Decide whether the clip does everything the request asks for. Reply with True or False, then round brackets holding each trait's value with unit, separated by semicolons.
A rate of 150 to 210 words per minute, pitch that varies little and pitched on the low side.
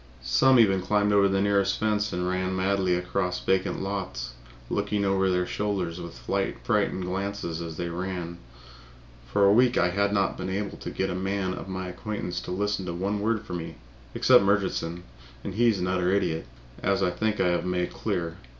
True (195 wpm; 2.1 semitones; 95 Hz)